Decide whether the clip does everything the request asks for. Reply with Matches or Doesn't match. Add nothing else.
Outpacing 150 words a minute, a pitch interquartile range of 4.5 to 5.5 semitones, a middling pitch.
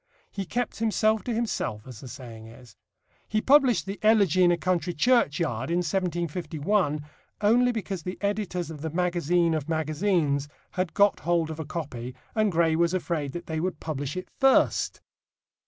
Matches